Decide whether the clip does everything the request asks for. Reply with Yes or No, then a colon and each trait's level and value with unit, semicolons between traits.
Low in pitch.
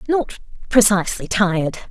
No: high, 210 Hz